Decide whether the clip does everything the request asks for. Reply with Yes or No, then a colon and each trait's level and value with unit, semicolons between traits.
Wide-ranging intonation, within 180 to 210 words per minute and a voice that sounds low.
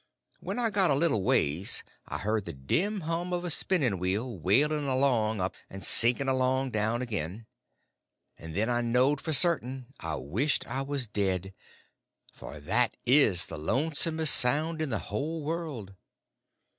No: wide, 6.9 semitones; average, 155 wpm; low, 125 Hz